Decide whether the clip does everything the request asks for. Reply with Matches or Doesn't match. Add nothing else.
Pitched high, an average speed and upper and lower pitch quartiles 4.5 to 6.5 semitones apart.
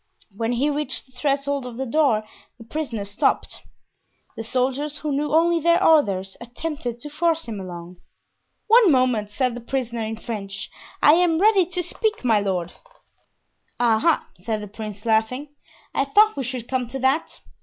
Matches